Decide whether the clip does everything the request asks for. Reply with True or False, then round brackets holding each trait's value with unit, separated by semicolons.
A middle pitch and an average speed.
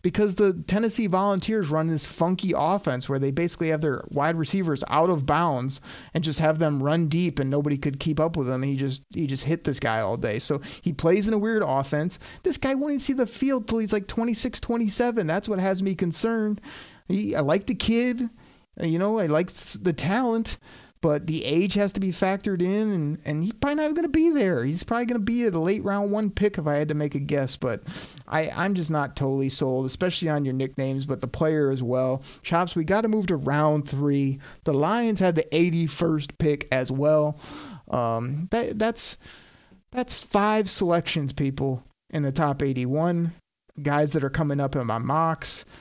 False (165 Hz; 210 wpm)